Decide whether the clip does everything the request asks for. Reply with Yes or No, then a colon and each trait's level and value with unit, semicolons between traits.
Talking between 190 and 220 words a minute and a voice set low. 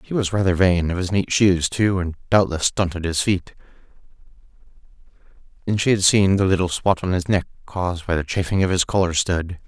Yes: average, 200 wpm; very low, 90 Hz